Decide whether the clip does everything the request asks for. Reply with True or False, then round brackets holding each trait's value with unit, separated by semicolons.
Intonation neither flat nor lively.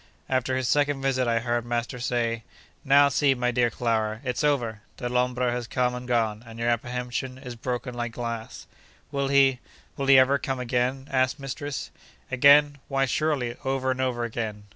False (2.1 semitones)